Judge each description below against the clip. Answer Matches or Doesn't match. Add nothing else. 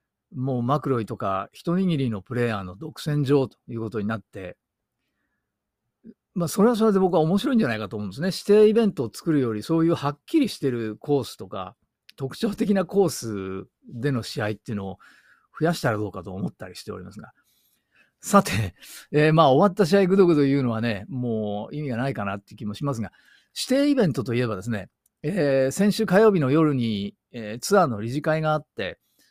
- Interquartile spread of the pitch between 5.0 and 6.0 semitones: Doesn't match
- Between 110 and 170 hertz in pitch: Matches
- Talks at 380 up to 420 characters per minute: Matches